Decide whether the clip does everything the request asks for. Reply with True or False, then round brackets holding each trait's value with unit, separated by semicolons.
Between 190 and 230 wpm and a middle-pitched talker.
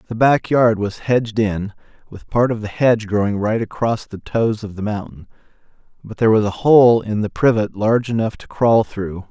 False (205 wpm; 110 Hz)